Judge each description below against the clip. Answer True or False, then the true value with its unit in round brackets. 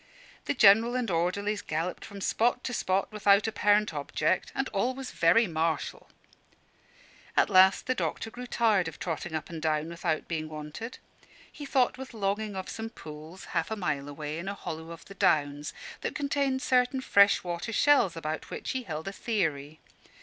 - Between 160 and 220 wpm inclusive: True (175 wpm)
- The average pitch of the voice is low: False (195 Hz)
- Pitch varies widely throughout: True (6.1 semitones)